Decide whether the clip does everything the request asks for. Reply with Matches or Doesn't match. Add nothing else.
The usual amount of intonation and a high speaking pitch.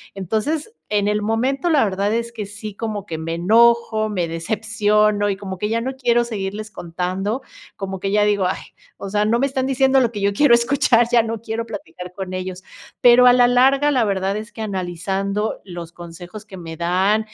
Matches